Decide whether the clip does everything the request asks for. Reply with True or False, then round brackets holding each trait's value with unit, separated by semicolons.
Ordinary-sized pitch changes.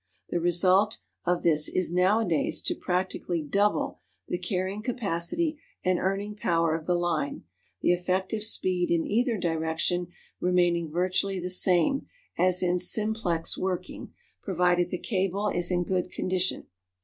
False (2.0 semitones)